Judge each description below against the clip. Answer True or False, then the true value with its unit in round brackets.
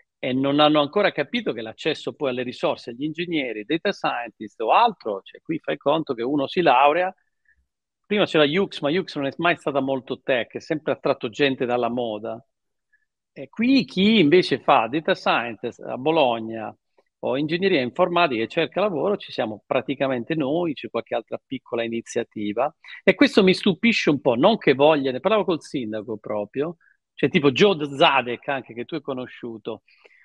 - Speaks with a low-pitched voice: False (145 Hz)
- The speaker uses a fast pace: True (175 wpm)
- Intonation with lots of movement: True (7.2 semitones)